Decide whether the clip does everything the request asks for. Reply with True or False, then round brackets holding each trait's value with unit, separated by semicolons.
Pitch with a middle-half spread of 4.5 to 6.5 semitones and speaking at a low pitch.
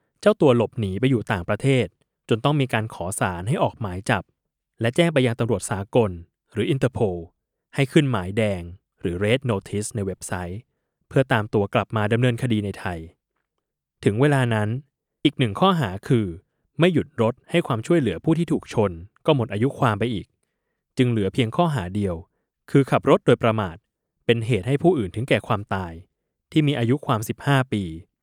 True (5.3 semitones; 115 Hz)